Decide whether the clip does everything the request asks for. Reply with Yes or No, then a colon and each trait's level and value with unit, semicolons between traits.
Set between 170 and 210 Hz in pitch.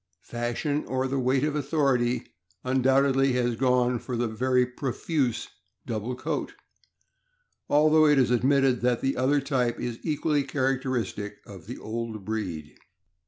No: low, 130 Hz